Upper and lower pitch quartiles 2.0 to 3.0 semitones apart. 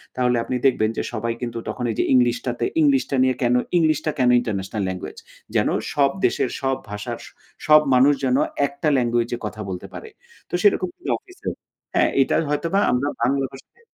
No: average, 3.6 semitones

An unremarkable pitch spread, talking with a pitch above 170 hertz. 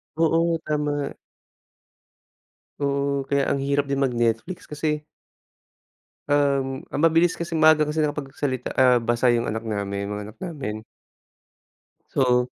No: average, 3.5 semitones; medium, 140 Hz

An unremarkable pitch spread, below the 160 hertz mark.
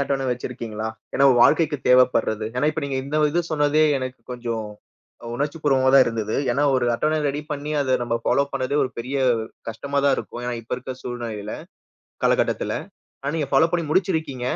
Yes: average, 3.2 semitones; low, 135 Hz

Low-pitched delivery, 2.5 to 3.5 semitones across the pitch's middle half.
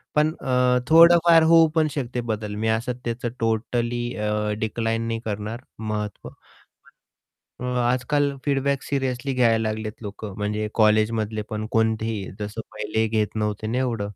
Yes: low, 115 Hz; average, 2.8 semitones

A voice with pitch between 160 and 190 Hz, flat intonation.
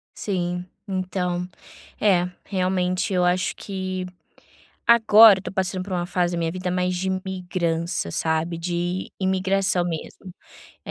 Yes: medium, 185 Hz; narrow, 1.3 semitones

